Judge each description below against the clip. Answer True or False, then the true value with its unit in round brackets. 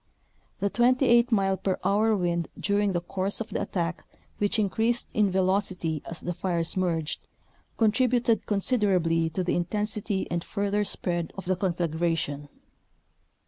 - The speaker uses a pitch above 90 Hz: True (190 Hz)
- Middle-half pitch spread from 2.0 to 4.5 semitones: True (3.5 semitones)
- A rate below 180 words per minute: True (140 wpm)